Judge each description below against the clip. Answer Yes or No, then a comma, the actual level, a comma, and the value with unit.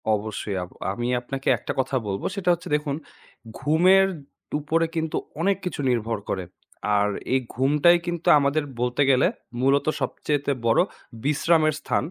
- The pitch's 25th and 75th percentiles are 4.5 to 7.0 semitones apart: Yes, average, 4.9 semitones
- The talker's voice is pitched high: No, medium, 140 Hz